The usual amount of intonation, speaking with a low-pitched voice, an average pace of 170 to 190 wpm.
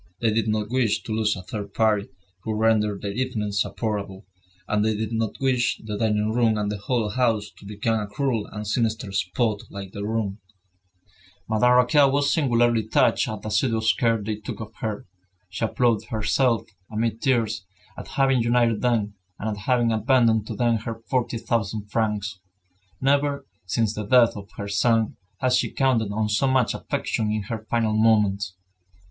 No: narrow, 2.2 semitones; low, 110 Hz; average, 175 wpm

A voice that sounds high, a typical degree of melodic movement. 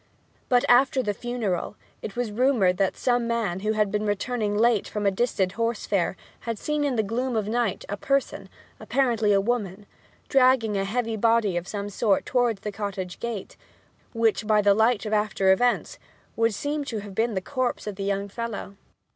Yes: high, 215 Hz; average, 3.2 semitones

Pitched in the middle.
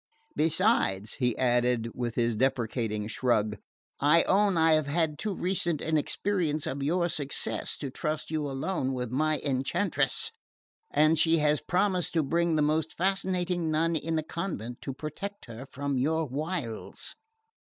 Yes: medium, 155 Hz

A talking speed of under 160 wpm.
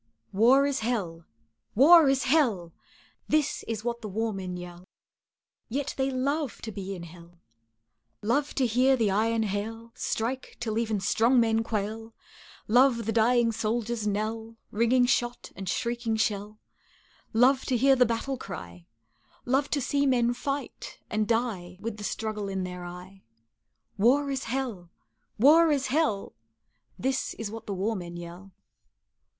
Yes: average, 150 wpm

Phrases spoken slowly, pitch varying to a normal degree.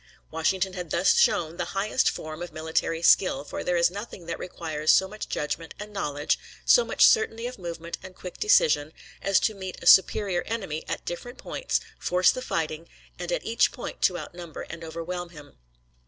No: average, 185 wpm; average, 3.4 semitones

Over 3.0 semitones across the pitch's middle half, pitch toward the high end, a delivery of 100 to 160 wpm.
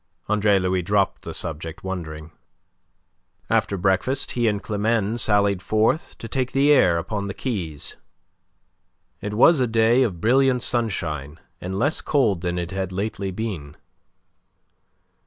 No: average, 4.2 semitones; low, 100 Hz; average, 140 wpm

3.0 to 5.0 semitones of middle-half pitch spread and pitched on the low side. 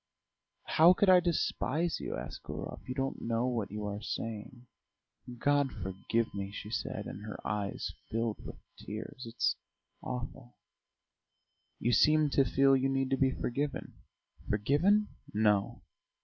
Yes: average, 4.6 semitones; low, 125 Hz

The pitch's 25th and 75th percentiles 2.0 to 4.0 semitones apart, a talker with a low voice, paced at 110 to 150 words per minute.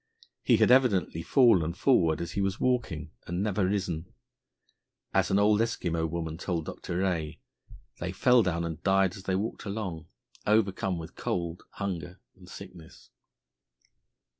Yes: average, 3.5 semitones; very low, 90 Hz; average, 145 wpm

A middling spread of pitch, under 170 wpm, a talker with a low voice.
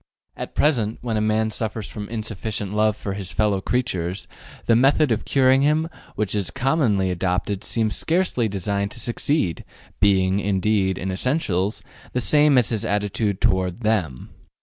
Yes: average, 3.7 semitones; average, 155 wpm; low, 105 Hz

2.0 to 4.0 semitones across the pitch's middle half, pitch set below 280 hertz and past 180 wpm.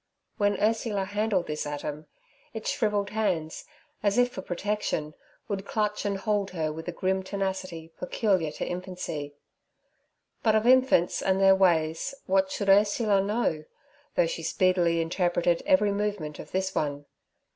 No: average, 3.7 semitones; high, 190 Hz; average, 145 wpm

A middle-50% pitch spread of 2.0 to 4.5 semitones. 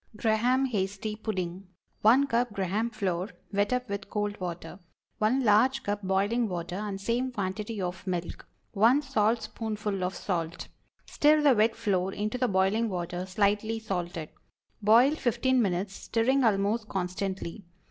Yes: average, 3.5 semitones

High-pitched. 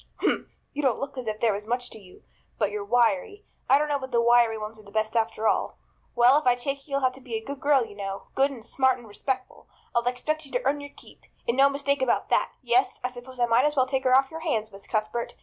Yes: very high, 250 Hz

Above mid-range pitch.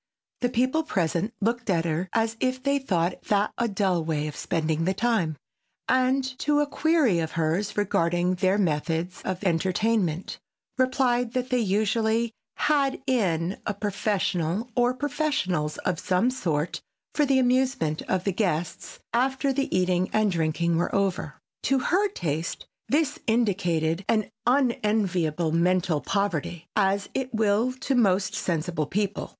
Yes: high, 200 Hz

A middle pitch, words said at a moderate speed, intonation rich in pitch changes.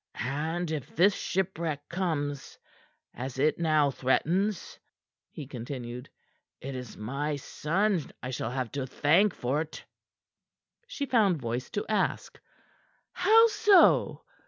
No: medium, 150 Hz; slow, 115 wpm; wide, 6.1 semitones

